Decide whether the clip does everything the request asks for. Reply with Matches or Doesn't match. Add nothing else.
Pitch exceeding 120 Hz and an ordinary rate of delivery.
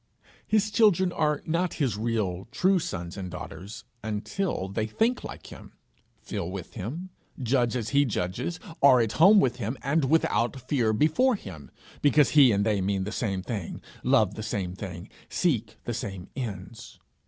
Doesn't match